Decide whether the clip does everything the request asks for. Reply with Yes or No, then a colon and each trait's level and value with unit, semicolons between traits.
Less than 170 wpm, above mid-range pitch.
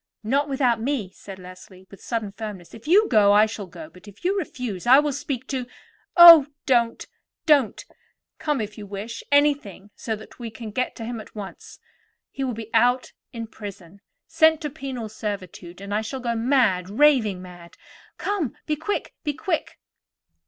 No: average, 175 wpm; high, 230 Hz